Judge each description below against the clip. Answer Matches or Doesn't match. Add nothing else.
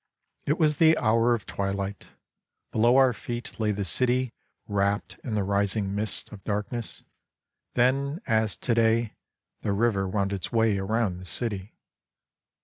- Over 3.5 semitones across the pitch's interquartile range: Doesn't match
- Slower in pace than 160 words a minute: Matches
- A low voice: Matches